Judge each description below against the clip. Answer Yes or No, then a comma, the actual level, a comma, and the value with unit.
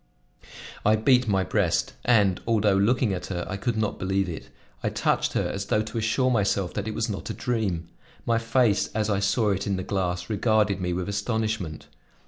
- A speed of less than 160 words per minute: No, average, 200 wpm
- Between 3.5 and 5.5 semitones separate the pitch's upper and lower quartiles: No, narrow, 2.6 semitones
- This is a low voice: Yes, low, 105 Hz